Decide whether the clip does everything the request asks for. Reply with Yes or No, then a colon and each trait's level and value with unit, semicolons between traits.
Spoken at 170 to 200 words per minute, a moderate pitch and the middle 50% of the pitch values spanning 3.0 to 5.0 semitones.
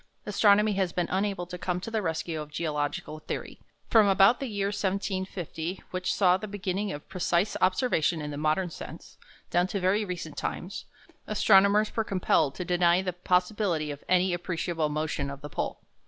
Yes: average, 175 wpm; medium, 180 Hz; average, 3.5 semitones